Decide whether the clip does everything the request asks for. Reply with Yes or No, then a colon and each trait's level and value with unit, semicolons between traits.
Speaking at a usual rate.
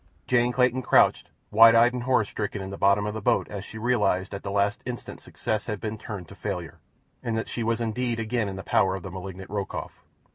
No: fast, 240 wpm